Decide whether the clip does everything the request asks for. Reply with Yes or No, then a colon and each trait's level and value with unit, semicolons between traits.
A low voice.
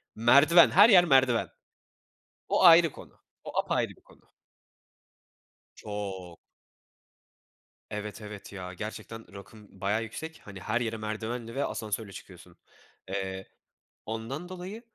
Yes: low, 110 Hz